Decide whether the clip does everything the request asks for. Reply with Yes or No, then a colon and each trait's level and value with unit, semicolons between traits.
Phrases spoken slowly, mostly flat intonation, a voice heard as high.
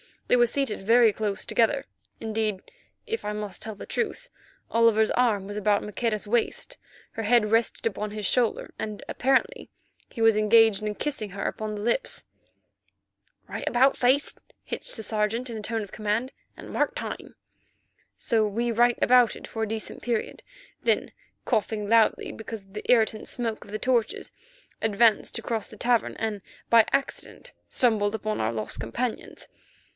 No: average, 160 wpm; narrow, 2.3 semitones; high, 220 Hz